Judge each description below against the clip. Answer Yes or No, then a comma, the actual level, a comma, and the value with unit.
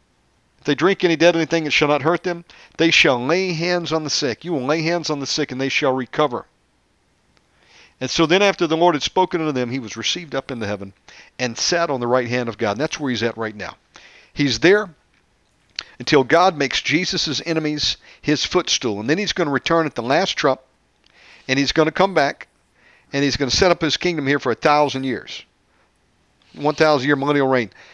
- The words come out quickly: Yes, fast, 220 wpm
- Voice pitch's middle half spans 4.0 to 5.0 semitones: Yes, average, 4.5 semitones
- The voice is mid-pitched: Yes, medium, 150 Hz